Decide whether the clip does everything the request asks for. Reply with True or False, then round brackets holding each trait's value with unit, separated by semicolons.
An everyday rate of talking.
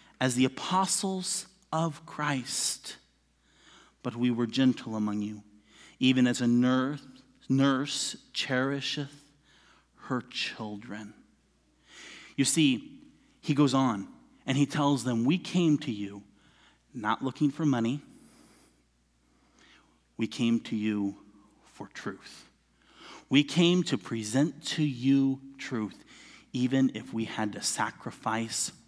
False (110 wpm)